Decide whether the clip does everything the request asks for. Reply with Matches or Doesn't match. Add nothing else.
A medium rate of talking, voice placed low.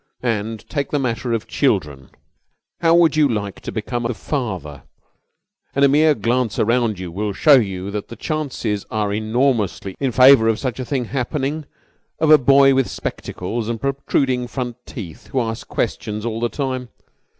Matches